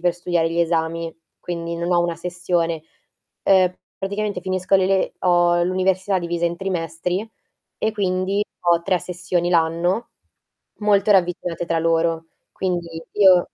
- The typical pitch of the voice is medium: Yes, medium, 175 Hz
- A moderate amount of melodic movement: No, narrow, 1.8 semitones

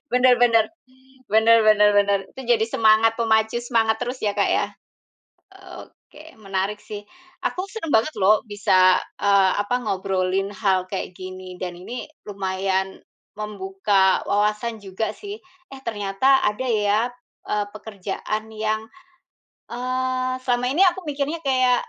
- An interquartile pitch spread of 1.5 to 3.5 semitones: No, average, 3.9 semitones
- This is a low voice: No, high, 215 Hz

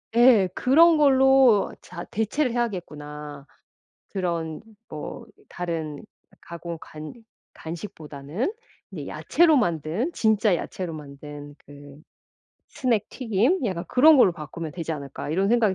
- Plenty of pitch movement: Yes, wide, 7.7 semitones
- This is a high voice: No, medium, 180 Hz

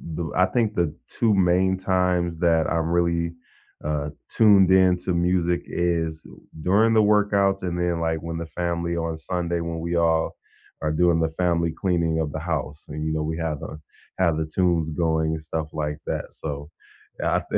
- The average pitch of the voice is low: Yes, very low, 85 Hz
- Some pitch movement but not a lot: No, narrow, 2.2 semitones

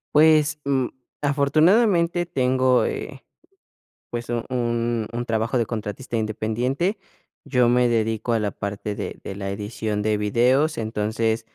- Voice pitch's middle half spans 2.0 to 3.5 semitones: No, average, 4.1 semitones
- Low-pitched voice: Yes, low, 120 Hz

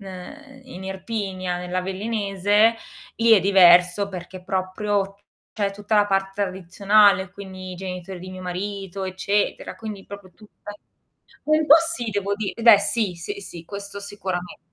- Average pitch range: No, narrow, 1.9 semitones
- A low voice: No, high, 195 Hz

